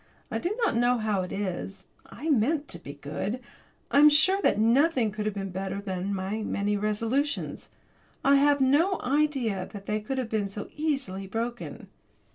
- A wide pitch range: Yes, wide, 6.0 semitones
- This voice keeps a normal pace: Yes, average, 175 wpm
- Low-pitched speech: No, high, 225 Hz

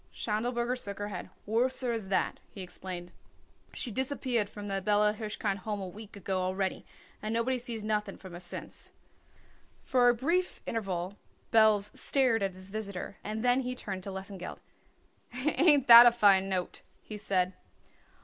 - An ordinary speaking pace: Yes, average, 160 wpm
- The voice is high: Yes, high, 210 Hz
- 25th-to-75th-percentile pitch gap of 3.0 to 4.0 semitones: Yes, average, 3.7 semitones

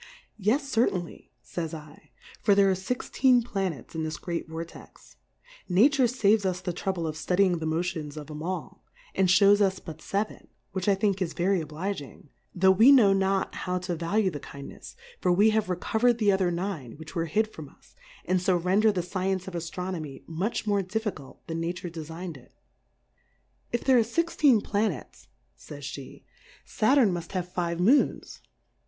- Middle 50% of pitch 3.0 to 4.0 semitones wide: Yes, average, 3.7 semitones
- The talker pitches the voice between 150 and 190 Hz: Yes, medium, 185 Hz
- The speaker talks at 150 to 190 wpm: Yes, average, 180 wpm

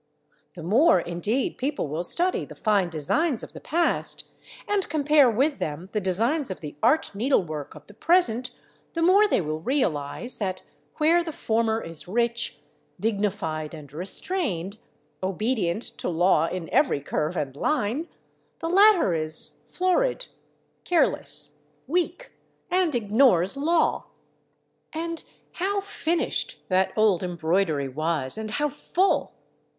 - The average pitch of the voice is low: No, high, 220 Hz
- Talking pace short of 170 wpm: Yes, slow, 135 wpm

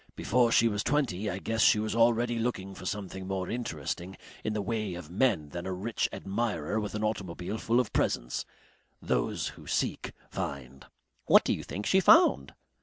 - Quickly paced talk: No, average, 180 wpm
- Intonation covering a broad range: No, average, 4.1 semitones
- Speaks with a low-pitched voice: Yes, low, 105 Hz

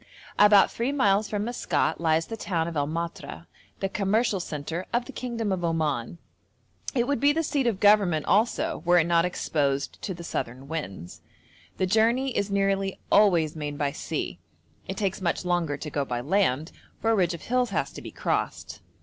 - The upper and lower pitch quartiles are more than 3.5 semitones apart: Yes, average, 5.1 semitones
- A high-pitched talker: No, medium, 180 Hz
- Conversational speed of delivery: Yes, average, 190 wpm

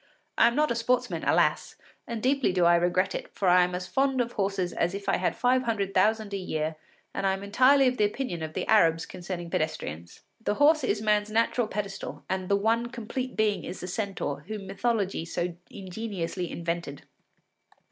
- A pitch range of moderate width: Yes, average, 4.4 semitones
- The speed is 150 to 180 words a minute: No, average, 200 wpm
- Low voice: No, high, 200 Hz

